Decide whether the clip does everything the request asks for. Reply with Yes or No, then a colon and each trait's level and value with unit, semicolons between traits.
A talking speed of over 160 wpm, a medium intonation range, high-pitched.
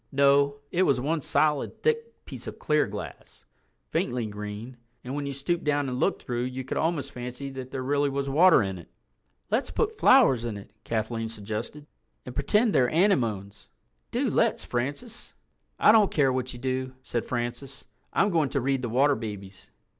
No: average, 180 wpm; average, 3.8 semitones; low, 135 Hz